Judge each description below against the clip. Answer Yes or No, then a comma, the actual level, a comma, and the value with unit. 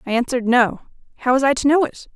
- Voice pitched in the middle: No, very high, 255 Hz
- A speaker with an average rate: No, fast, 250 wpm